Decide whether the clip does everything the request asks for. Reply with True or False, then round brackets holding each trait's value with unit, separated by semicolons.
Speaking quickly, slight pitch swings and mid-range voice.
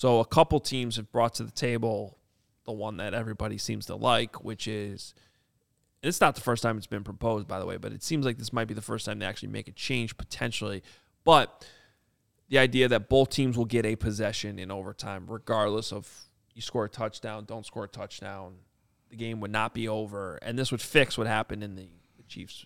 False (215 wpm; 2.3 semitones; 110 Hz)